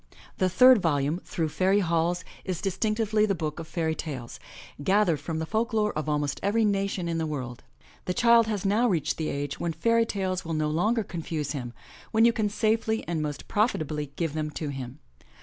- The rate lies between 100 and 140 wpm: No, average, 200 wpm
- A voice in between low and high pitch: Yes, medium, 175 Hz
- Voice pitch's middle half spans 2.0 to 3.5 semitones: No, wide, 5.5 semitones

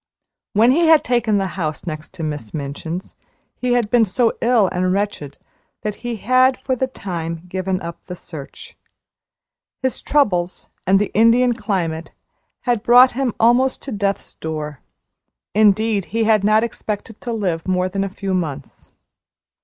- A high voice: Yes, high, 205 Hz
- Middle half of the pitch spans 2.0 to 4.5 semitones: No, average, 5.2 semitones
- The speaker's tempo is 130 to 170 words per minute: Yes, average, 160 wpm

